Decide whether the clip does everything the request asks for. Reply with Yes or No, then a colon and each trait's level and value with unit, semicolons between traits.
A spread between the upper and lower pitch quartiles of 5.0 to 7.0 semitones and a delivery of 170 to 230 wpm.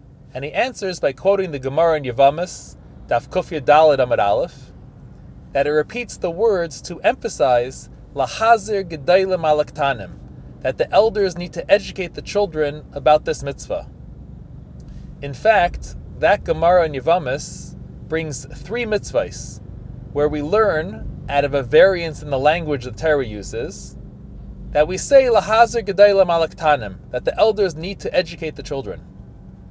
No: average, 5.3 semitones; slow, 135 wpm